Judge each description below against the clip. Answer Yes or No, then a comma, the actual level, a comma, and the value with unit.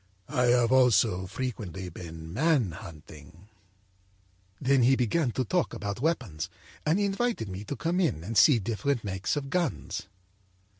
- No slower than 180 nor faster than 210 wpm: No, average, 150 wpm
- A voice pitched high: No, low, 120 Hz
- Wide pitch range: Yes, wide, 7.1 semitones